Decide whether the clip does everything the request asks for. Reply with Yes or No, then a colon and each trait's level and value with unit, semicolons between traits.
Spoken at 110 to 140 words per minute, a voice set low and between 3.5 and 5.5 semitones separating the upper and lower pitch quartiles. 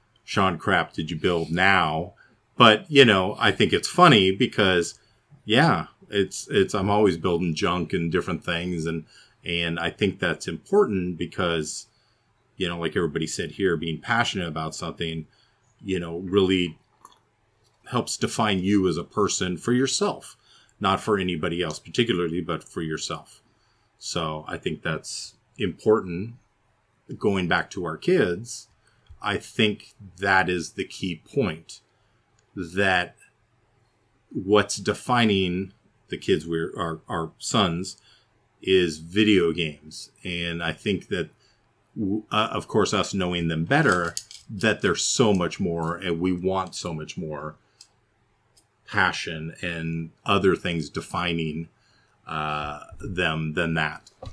Yes: slow, 135 wpm; very low, 95 Hz; average, 4.9 semitones